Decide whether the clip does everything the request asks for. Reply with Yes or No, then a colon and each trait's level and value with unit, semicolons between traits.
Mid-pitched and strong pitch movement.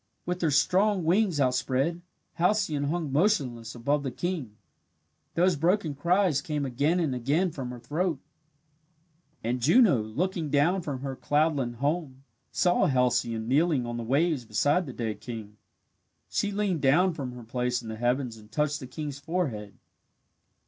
Yes: medium, 145 Hz; wide, 5.7 semitones